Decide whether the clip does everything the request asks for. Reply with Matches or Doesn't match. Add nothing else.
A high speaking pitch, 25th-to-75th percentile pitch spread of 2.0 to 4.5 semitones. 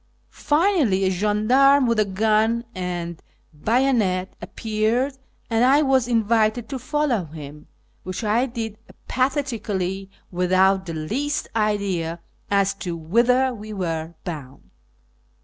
Doesn't match